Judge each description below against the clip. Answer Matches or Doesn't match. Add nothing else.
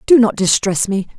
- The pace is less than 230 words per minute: Matches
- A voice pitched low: Doesn't match